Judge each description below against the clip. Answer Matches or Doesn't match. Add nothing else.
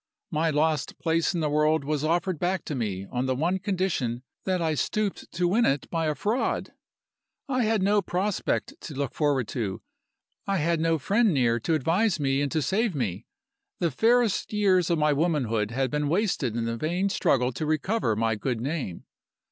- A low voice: Doesn't match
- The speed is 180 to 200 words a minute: Matches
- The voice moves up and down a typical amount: Doesn't match